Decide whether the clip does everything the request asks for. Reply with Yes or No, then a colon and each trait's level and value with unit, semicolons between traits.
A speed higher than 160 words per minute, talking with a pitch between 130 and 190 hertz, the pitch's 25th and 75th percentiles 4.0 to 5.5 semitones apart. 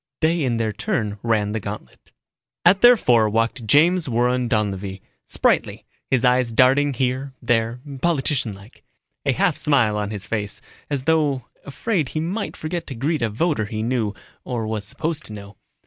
No: average, 170 wpm; low, 120 Hz; average, 5.1 semitones